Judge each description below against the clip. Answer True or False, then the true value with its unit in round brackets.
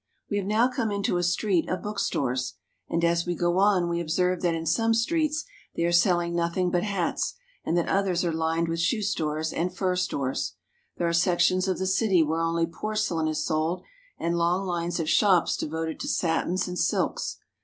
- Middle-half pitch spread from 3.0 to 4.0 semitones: False (2.4 semitones)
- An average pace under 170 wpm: False (195 wpm)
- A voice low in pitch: False (175 Hz)